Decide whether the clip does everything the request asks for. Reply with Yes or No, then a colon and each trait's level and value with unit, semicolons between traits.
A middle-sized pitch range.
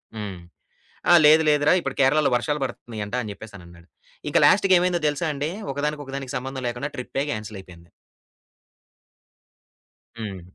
No: wide, 5.8 semitones